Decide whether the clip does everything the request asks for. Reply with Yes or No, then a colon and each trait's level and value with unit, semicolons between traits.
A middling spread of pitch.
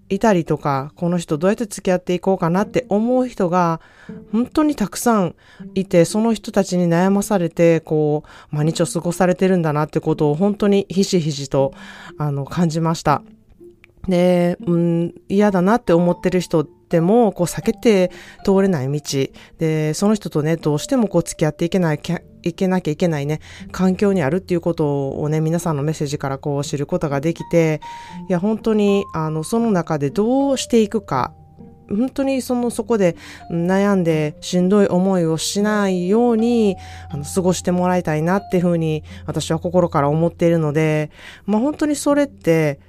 Yes: average, 4.2 semitones